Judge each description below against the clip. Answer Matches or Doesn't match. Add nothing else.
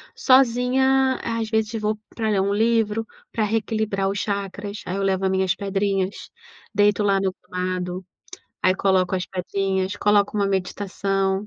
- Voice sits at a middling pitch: Doesn't match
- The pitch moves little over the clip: Matches